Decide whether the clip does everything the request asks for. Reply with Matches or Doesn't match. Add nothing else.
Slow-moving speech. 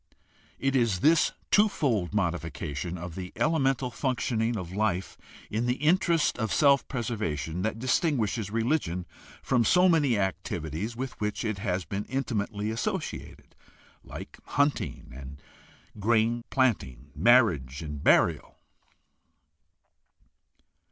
Matches